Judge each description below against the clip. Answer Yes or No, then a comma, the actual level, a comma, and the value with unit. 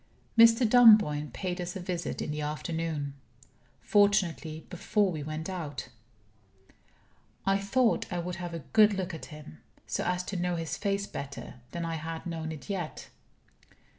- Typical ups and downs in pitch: Yes, average, 4.0 semitones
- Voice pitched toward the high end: No, medium, 175 Hz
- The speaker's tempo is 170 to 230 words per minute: No, average, 160 wpm